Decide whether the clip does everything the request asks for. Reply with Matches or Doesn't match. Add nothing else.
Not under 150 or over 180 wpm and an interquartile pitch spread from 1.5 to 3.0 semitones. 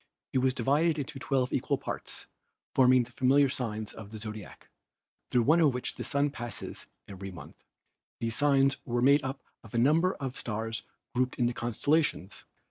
Doesn't match